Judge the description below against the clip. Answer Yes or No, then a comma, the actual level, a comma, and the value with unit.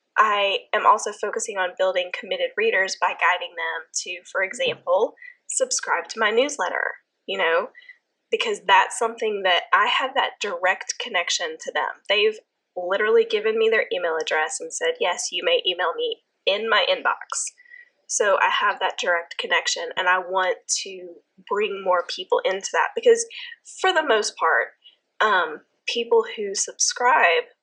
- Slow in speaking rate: No, average, 155 wpm